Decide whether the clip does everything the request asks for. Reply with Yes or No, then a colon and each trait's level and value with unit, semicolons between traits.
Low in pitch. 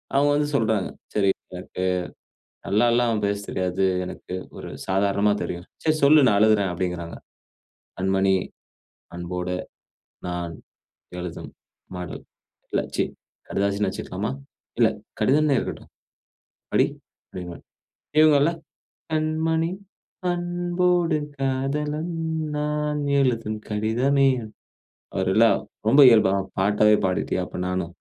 Yes: low, 110 Hz